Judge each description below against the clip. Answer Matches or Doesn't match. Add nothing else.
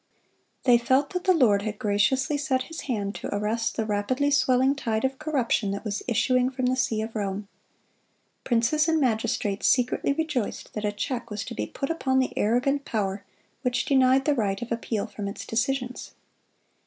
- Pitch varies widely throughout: Doesn't match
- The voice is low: Doesn't match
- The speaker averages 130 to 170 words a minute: Doesn't match